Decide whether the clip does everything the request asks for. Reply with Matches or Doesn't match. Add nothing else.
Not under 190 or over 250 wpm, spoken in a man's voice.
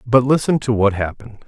Matches